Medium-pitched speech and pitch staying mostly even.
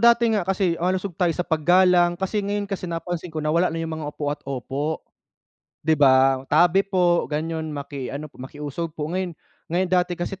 No: medium, 170 Hz; average, 3.3 semitones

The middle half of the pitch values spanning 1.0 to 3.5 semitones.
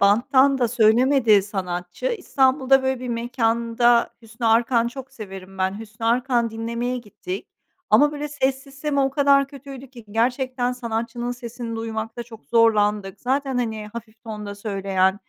Yes: average, 3.2 semitones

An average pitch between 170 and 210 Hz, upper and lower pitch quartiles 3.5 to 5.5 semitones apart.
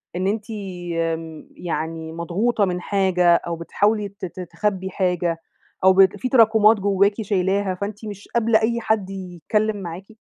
No: high, 190 Hz; average, 3.1 semitones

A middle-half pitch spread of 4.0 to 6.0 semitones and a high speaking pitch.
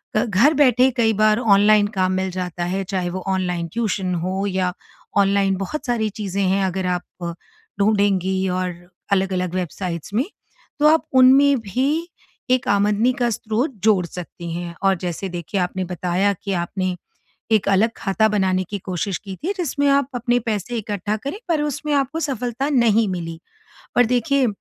Yes: average, 4.6 semitones; high, 200 Hz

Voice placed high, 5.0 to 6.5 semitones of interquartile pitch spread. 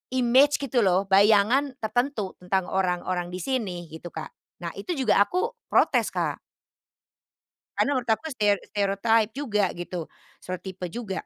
Yes: high, 210 Hz; wide, 5.4 semitones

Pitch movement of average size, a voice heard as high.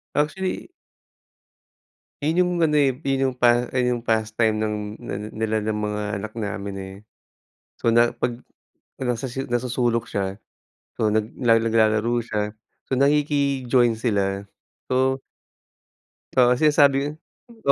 No: average, 3.4 semitones; low, 120 Hz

